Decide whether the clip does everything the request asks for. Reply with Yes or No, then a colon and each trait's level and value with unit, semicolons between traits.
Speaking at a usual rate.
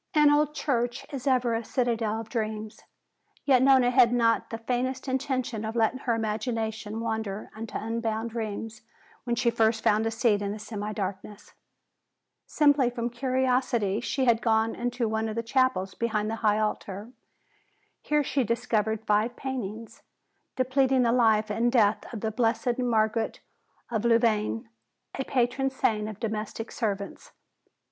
Yes: average, 155 wpm